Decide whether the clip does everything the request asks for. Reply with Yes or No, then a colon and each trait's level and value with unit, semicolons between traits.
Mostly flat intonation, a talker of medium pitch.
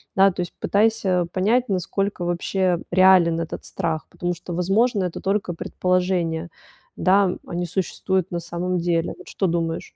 Yes: narrow, 2.0 semitones; medium, 180 Hz